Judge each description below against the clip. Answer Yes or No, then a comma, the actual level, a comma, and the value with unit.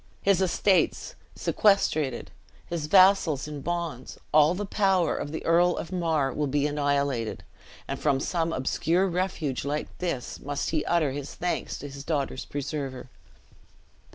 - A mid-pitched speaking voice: Yes, medium, 155 Hz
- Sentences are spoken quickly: No, average, 140 wpm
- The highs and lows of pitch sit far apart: No, average, 3.7 semitones